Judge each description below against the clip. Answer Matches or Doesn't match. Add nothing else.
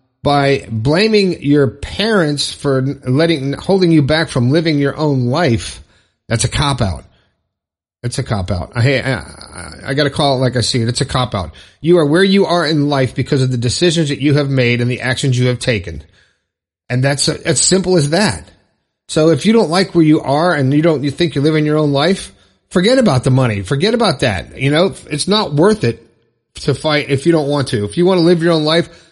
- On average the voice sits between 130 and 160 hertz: Matches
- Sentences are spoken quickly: Matches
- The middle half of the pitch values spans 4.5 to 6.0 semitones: Matches